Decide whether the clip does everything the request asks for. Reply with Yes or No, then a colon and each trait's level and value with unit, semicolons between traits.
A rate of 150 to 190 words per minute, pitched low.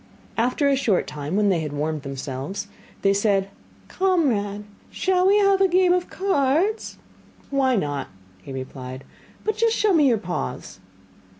No: average, 155 wpm; high, 220 Hz